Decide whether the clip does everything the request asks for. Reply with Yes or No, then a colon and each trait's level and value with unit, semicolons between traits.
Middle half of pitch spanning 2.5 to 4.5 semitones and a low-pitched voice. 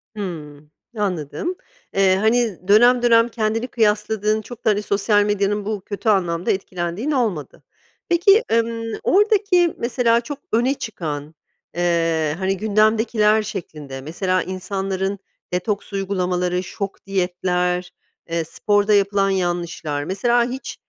No: average, 4.0 semitones; high, 200 Hz